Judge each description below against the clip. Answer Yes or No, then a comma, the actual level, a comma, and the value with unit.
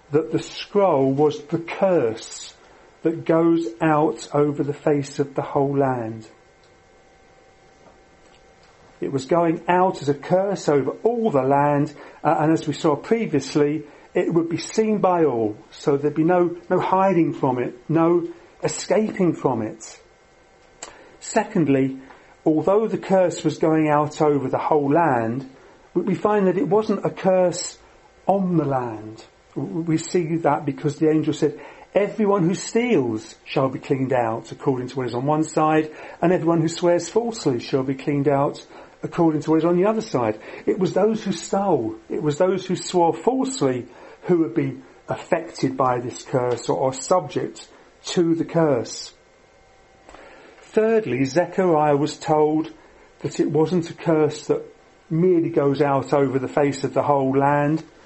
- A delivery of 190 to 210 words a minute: No, average, 160 wpm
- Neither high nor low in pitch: Yes, medium, 155 Hz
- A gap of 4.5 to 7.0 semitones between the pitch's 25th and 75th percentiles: No, average, 3.8 semitones